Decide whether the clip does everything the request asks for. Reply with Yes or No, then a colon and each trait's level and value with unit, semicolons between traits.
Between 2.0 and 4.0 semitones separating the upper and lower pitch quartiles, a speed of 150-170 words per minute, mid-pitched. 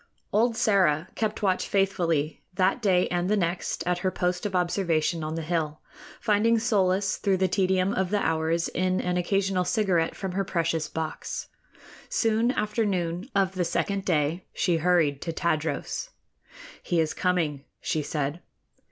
Yes: average, 3.1 semitones; average, 160 wpm; medium, 180 Hz